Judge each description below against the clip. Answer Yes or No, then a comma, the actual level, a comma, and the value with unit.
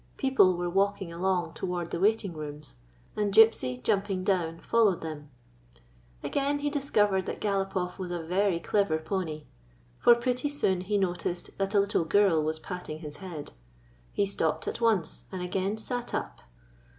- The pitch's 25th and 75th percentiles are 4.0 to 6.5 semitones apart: No, average, 3.6 semitones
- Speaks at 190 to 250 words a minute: No, average, 160 wpm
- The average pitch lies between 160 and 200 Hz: Yes, high, 190 Hz